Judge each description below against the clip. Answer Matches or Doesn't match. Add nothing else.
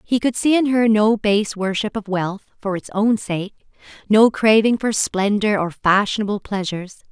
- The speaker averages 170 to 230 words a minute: Matches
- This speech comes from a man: Doesn't match